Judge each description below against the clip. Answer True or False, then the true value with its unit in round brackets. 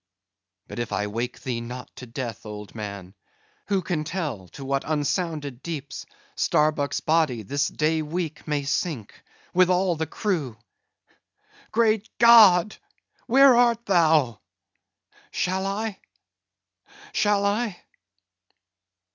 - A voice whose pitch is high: False (155 Hz)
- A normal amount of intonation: False (7.0 semitones)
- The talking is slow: True (115 wpm)